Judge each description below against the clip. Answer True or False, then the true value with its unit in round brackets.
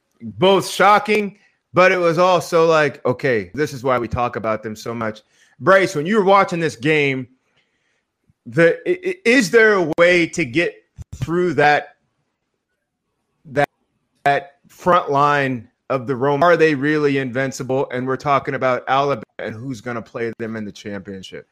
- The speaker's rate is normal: True (160 wpm)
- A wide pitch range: True (5.8 semitones)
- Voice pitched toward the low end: False (145 Hz)